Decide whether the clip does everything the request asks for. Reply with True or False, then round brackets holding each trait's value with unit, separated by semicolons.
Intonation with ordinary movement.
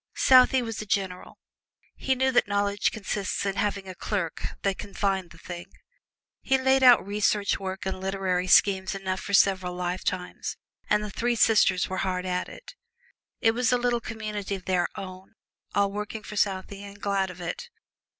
False (2.3 semitones)